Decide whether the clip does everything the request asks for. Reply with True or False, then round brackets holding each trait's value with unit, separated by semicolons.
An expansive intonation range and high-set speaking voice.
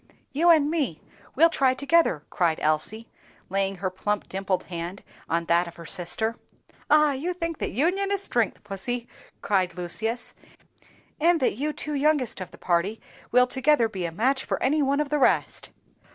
True (8.1 semitones; 235 Hz)